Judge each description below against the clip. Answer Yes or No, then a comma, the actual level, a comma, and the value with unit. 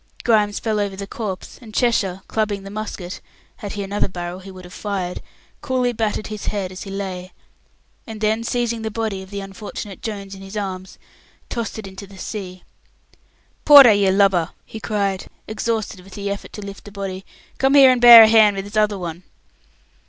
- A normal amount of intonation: No, narrow, 2.3 semitones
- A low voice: No, high, 200 Hz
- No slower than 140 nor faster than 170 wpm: No, average, 190 wpm